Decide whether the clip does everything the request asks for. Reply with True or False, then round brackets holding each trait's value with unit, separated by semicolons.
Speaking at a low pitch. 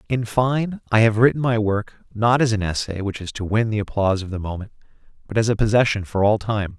True (110 Hz)